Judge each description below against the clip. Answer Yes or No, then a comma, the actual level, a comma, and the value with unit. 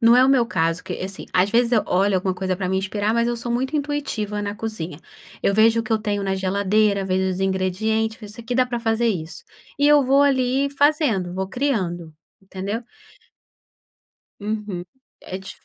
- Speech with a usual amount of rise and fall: Yes, average, 4.0 semitones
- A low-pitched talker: No, high, 210 Hz